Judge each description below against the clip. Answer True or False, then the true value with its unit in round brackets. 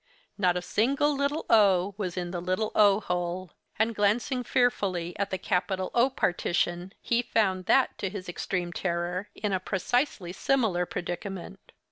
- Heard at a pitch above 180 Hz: True (190 Hz)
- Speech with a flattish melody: False (3.7 semitones)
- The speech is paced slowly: False (155 wpm)